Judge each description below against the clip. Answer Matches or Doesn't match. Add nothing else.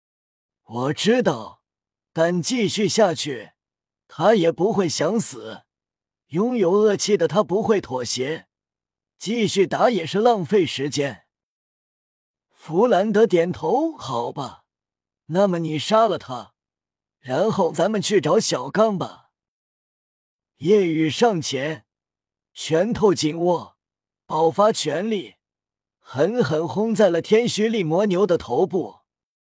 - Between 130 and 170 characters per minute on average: Matches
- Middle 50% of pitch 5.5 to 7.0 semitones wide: Matches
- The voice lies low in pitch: Doesn't match